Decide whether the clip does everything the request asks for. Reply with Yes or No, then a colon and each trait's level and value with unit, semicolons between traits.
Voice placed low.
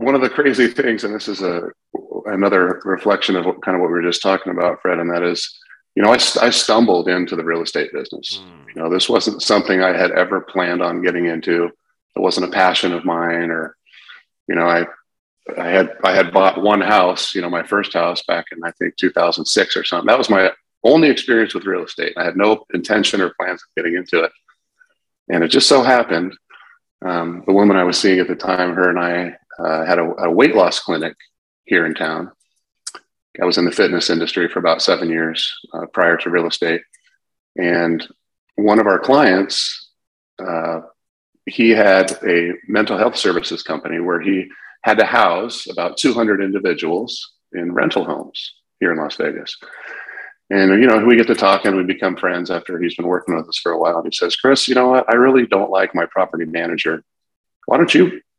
Yes: very low, 90 Hz